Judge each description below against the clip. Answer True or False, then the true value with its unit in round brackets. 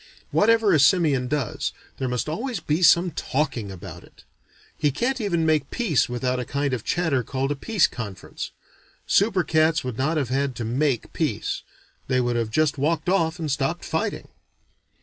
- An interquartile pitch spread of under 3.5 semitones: False (4.7 semitones)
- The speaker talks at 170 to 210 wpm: True (175 wpm)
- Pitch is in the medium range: True (145 Hz)